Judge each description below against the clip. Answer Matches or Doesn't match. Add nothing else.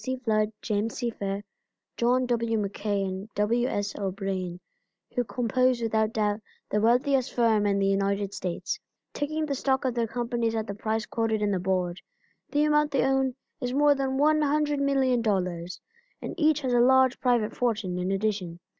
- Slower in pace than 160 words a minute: Doesn't match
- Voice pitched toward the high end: Matches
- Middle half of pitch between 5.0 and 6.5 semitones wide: Doesn't match